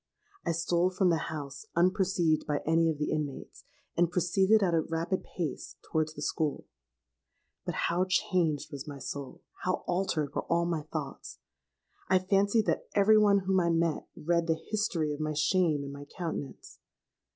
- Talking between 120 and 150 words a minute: No, average, 165 wpm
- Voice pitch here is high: No, medium, 170 Hz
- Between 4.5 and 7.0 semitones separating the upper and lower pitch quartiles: No, average, 3.3 semitones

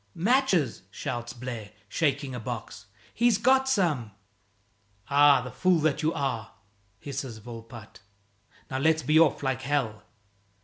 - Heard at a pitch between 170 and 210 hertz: No, low, 135 Hz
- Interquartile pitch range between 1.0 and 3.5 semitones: No, average, 5.0 semitones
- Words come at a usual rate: No, slow, 130 wpm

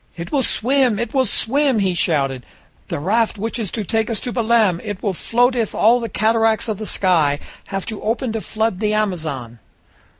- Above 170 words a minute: Yes, average, 200 wpm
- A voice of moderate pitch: No, high, 215 Hz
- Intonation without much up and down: No, average, 3.8 semitones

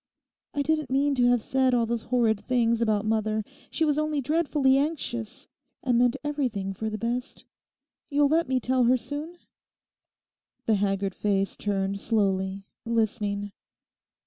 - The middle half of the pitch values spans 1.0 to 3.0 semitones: No, average, 4.7 semitones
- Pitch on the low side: No, high, 240 Hz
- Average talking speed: Yes, average, 145 wpm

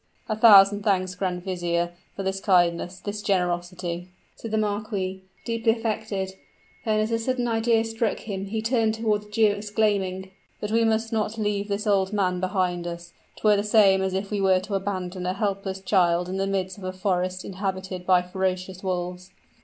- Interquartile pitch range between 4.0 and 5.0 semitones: No, narrow, 2.6 semitones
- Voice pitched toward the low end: No, high, 195 Hz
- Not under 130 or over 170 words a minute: No, average, 185 wpm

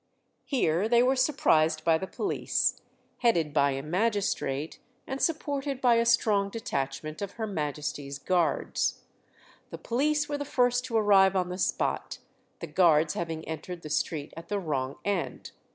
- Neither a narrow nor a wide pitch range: No, wide, 7.2 semitones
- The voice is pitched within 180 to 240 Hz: Yes, high, 190 Hz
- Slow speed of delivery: No, average, 155 wpm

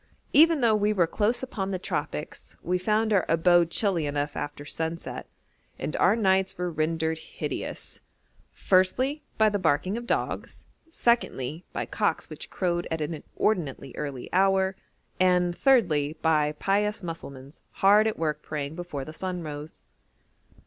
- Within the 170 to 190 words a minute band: No, average, 150 wpm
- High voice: No, medium, 175 Hz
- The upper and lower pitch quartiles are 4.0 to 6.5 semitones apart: Yes, average, 4.8 semitones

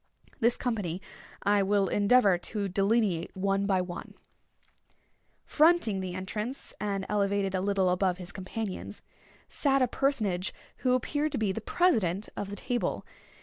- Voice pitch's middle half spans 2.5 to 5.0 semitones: Yes, average, 3.5 semitones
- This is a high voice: Yes, high, 200 Hz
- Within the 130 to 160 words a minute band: Yes, average, 145 wpm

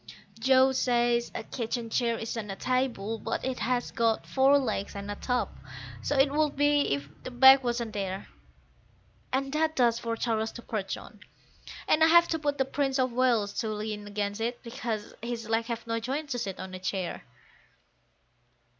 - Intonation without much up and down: No, average, 3.4 semitones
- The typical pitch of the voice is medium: No, high, 235 Hz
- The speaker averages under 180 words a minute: No, average, 185 wpm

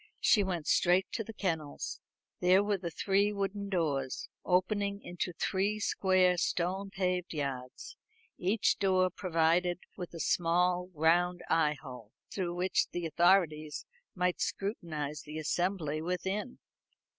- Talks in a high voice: No, medium, 180 Hz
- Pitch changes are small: No, average, 3.0 semitones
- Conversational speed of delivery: No, slow, 130 wpm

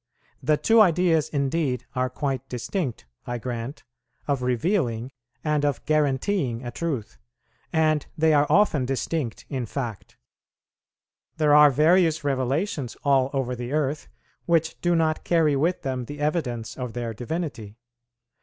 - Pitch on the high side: No, medium, 140 Hz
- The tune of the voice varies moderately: Yes, average, 4.1 semitones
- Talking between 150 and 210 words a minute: No, slow, 135 wpm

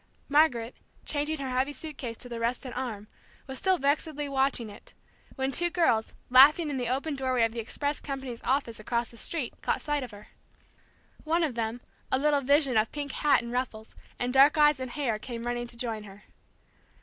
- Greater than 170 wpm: Yes, average, 195 wpm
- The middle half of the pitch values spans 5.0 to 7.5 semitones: No, average, 3.7 semitones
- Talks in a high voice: Yes, very high, 260 Hz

